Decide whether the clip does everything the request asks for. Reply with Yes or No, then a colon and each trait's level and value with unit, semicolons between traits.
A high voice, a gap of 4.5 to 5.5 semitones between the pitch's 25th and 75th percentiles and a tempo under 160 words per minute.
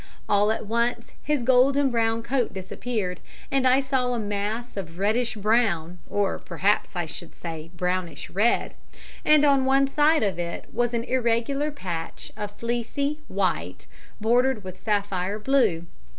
Yes: high, 225 Hz; average, 5.0 semitones; average, 150 wpm